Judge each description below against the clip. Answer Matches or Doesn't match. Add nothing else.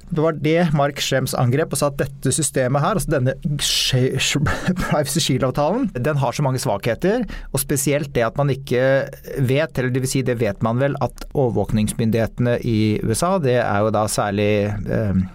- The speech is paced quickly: Doesn't match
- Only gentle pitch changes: Doesn't match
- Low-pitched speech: Matches